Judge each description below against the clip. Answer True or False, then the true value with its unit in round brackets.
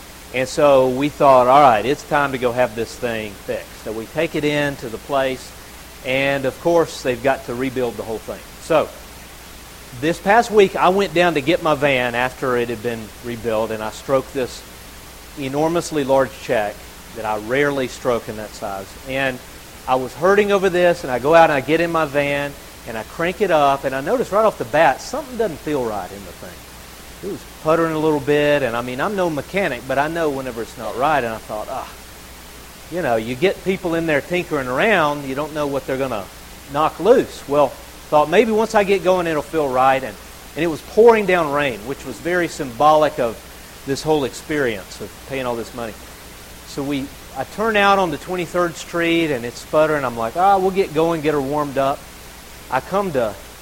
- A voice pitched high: False (140 Hz)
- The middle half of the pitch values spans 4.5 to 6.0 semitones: True (5.1 semitones)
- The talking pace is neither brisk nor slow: False (220 wpm)